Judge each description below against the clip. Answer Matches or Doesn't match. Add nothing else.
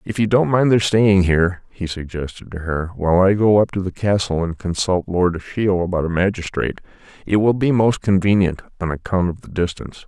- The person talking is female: Doesn't match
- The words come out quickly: Matches